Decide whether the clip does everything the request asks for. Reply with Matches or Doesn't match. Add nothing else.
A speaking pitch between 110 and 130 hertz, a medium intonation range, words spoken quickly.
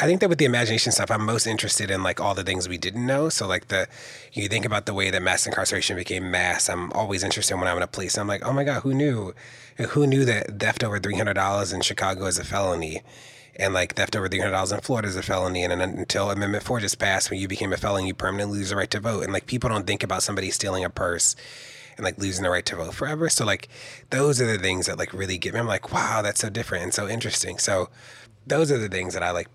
Doesn't match